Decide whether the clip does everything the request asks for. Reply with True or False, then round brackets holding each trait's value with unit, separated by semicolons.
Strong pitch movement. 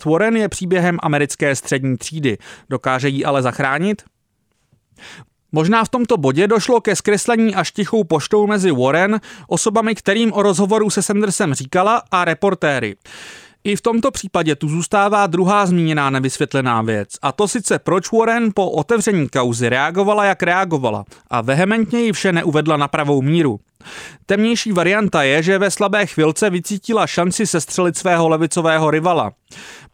True (6.3 semitones)